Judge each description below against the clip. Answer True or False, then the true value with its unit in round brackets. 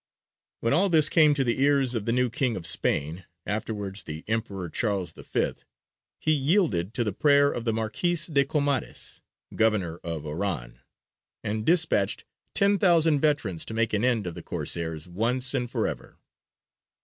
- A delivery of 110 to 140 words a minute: False (165 wpm)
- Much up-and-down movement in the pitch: True (6.9 semitones)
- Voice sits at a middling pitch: False (115 Hz)